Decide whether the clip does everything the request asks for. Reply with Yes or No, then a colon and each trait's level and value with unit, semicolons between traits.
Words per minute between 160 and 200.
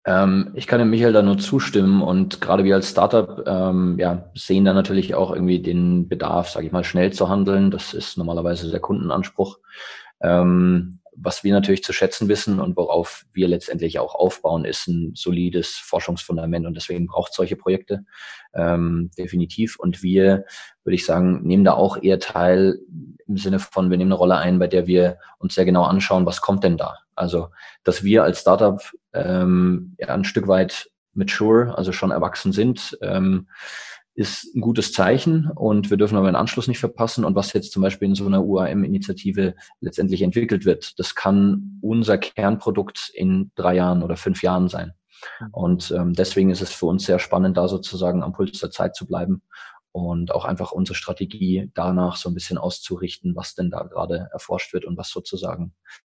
Yes: average, 185 wpm